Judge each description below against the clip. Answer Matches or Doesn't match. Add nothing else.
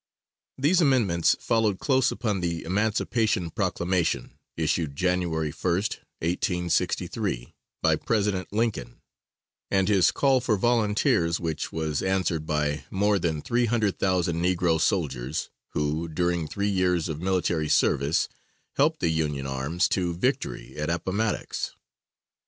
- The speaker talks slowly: Matches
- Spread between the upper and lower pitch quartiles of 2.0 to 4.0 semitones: Doesn't match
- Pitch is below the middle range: Matches